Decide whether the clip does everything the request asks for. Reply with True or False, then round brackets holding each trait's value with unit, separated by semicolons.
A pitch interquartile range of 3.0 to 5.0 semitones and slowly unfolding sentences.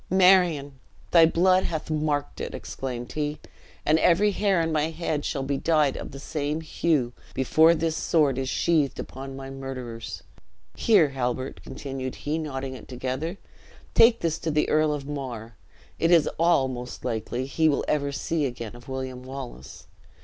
False (3.6 semitones; 165 wpm)